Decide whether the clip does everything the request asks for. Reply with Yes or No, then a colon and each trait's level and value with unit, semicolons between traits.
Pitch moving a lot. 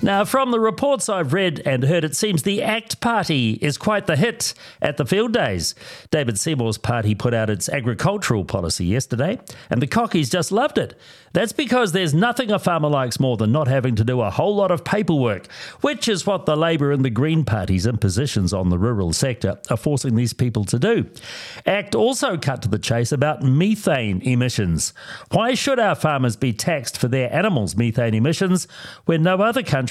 Yes: wide, 8.5 semitones